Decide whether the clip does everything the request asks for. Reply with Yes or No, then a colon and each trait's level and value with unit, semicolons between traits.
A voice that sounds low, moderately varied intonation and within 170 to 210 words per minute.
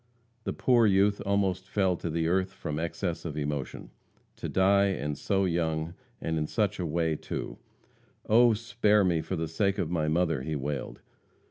Yes: very low, 85 Hz; average, 3.9 semitones; average, 175 wpm